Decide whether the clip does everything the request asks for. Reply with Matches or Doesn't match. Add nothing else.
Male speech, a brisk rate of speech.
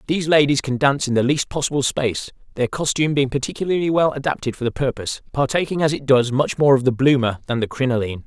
Matches